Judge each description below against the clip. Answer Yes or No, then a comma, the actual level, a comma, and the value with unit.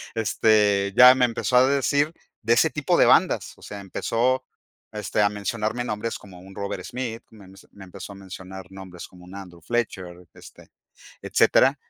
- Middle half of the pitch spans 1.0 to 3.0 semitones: No, average, 3.9 semitones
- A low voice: Yes, low, 105 Hz